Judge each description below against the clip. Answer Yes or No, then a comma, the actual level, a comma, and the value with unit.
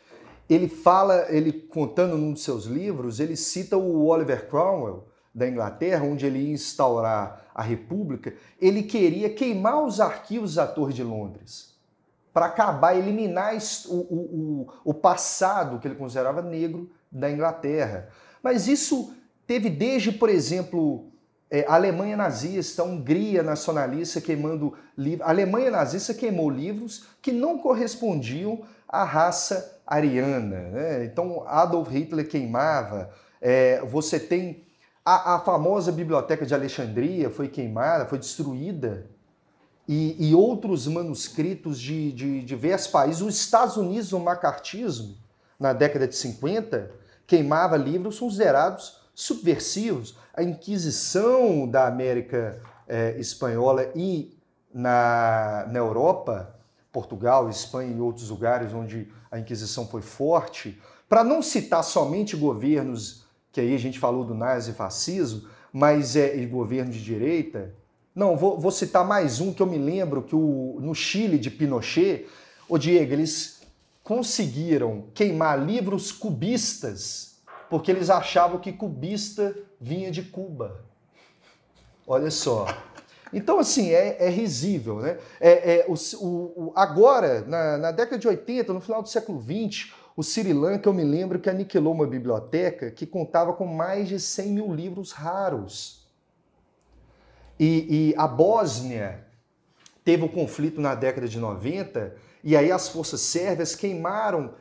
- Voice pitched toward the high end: No, medium, 160 Hz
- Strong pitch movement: Yes, wide, 6.0 semitones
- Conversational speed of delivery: Yes, average, 135 wpm